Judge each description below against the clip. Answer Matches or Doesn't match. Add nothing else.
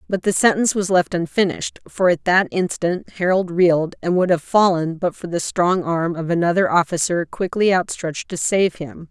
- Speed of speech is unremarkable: Matches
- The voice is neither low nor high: Matches